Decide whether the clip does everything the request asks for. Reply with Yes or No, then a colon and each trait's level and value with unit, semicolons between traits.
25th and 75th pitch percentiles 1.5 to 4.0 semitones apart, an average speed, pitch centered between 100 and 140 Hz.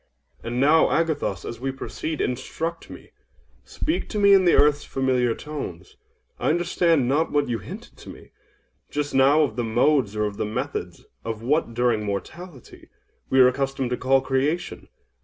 No: average, 4.5 semitones; average, 165 wpm; low, 135 Hz